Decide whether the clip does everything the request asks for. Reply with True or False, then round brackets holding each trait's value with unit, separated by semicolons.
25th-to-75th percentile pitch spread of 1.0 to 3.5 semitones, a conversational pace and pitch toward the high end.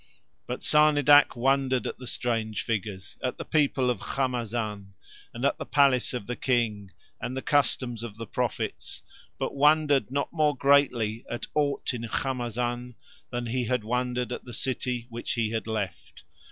False (2.9 semitones; 165 wpm; 125 Hz)